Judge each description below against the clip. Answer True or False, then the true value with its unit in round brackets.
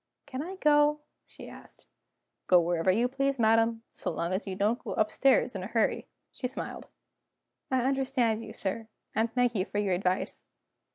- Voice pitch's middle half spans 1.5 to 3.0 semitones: False (5.1 semitones)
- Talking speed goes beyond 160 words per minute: True (175 wpm)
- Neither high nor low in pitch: False (230 Hz)